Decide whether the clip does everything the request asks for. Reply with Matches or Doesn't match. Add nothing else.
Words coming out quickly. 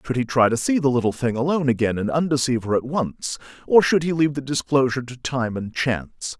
Matches